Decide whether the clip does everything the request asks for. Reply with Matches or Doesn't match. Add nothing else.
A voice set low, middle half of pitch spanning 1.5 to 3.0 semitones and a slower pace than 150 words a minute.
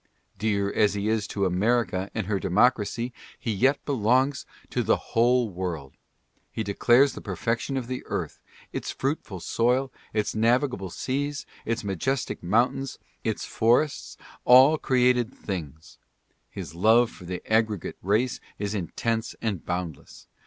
Doesn't match